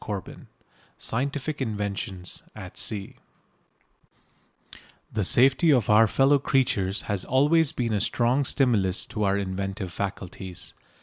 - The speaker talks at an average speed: No, slow, 120 wpm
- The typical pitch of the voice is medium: No, low, 105 Hz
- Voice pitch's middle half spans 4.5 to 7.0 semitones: Yes, wide, 5.4 semitones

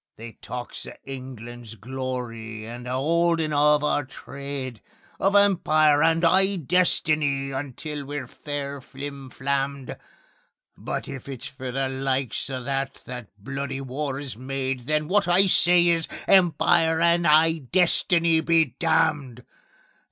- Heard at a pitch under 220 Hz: Yes, medium, 140 Hz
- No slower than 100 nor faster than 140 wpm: Yes, slow, 135 wpm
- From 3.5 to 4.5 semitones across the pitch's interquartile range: Yes, average, 3.8 semitones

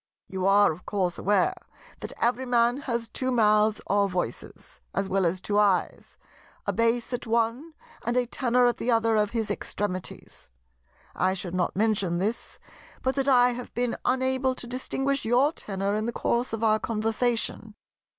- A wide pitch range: No, average, 3.3 semitones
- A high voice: Yes, high, 225 Hz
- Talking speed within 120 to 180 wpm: Yes, average, 165 wpm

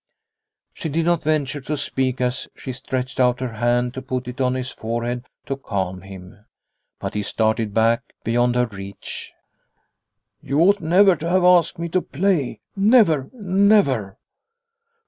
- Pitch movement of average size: No, wide, 5.9 semitones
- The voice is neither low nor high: No, low, 130 Hz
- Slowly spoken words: No, average, 160 wpm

